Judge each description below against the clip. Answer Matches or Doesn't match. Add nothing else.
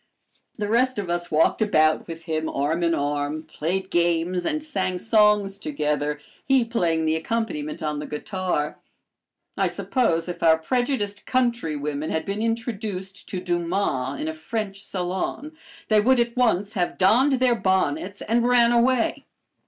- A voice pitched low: Doesn't match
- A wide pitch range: Matches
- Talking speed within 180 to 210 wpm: Doesn't match